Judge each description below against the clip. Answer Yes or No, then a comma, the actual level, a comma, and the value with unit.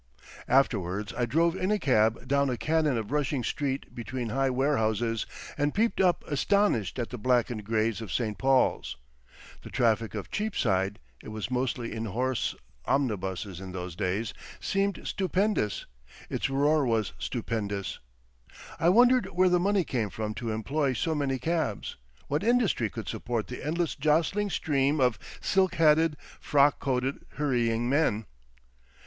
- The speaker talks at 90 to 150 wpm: Yes, average, 145 wpm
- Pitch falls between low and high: No, low, 130 Hz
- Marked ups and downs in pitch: Yes, wide, 5.9 semitones